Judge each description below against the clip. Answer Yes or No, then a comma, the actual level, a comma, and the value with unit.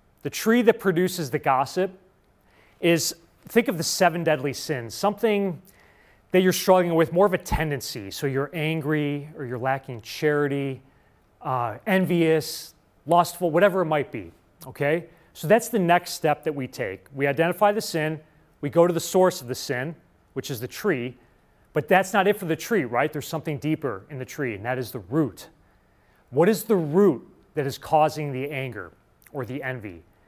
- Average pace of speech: Yes, average, 180 wpm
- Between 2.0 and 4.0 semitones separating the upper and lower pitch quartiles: No, average, 4.8 semitones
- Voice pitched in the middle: Yes, medium, 155 Hz